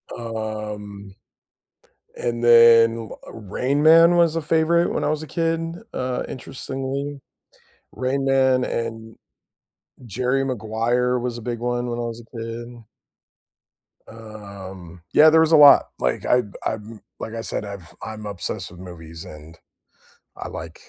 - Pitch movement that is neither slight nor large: Yes, average, 3.9 semitones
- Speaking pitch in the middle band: No, low, 120 Hz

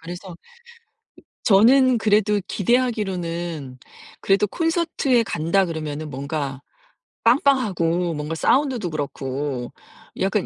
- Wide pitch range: Yes, wide, 6.9 semitones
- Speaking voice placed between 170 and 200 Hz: Yes, medium, 185 Hz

